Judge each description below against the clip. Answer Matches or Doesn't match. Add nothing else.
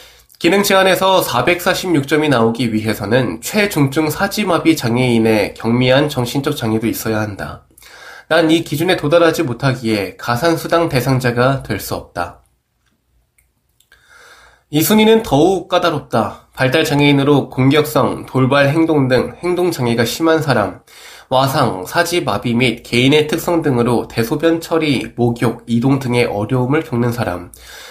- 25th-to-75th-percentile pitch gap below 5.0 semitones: Doesn't match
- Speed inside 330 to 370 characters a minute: Doesn't match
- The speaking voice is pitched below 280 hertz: Matches